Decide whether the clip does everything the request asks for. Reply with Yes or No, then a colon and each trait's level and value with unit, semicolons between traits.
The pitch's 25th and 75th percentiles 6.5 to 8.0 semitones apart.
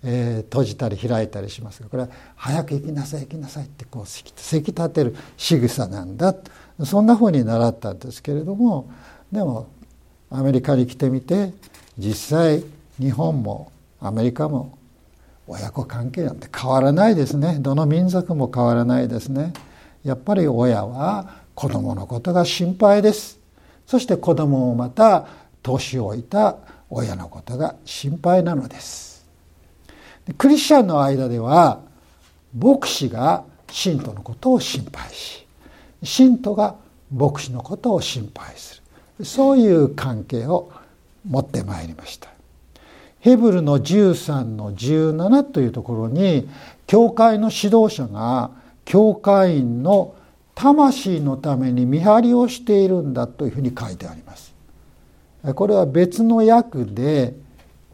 Yes: wide, 7.1 semitones